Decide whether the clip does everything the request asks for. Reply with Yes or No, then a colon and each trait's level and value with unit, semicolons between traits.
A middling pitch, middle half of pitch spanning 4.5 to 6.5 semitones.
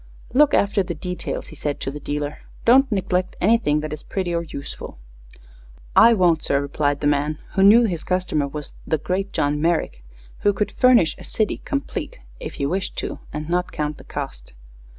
Yes: medium, 170 Hz; average, 5.2 semitones